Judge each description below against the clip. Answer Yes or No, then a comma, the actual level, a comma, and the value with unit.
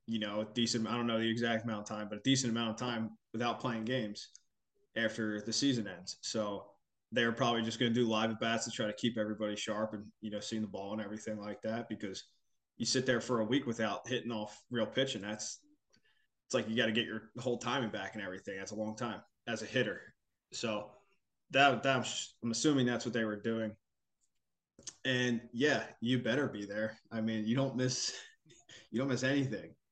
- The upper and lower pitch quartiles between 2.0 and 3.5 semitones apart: Yes, narrow, 2.5 semitones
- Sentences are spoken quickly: Yes, fast, 215 wpm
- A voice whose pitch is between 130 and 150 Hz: No, low, 115 Hz